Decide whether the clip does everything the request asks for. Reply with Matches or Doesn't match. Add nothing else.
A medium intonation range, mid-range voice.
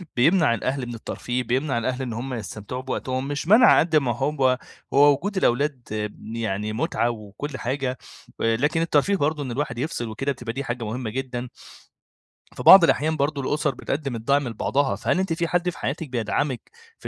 Doesn't match